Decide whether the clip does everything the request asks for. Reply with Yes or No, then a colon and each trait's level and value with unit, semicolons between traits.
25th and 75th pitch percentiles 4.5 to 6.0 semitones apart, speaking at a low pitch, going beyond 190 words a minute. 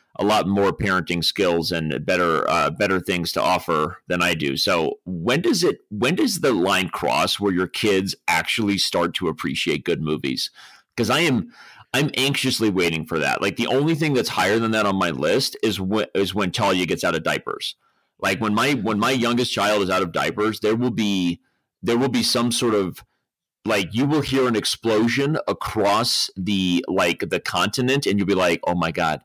Yes: average, 4.9 semitones; low, 105 Hz; fast, 205 wpm